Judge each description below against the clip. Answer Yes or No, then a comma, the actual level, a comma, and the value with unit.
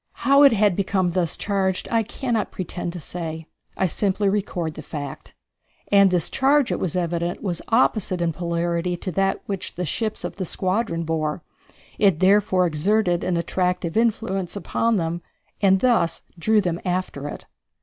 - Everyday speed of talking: Yes, average, 165 wpm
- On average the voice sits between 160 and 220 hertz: Yes, medium, 185 Hz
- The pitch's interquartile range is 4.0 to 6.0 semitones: No, average, 3.3 semitones